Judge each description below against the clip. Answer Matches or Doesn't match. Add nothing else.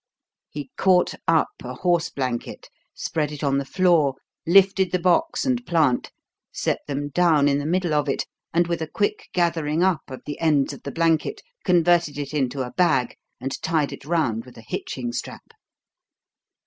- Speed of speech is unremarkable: Matches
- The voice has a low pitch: Doesn't match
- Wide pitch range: Doesn't match